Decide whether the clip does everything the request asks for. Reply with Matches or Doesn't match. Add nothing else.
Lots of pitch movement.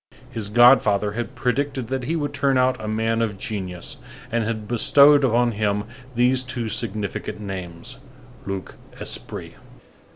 Doesn't match